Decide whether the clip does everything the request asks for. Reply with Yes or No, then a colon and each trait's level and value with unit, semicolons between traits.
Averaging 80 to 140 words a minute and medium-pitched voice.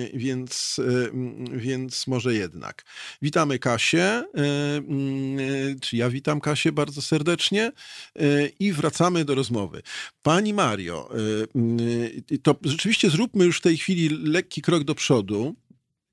Yes: slow, 110 wpm; medium, 145 Hz